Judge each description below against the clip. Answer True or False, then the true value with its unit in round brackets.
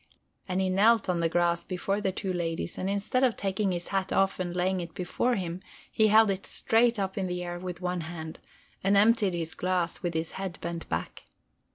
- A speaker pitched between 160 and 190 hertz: True (185 Hz)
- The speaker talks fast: True (215 wpm)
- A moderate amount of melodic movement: False (2.3 semitones)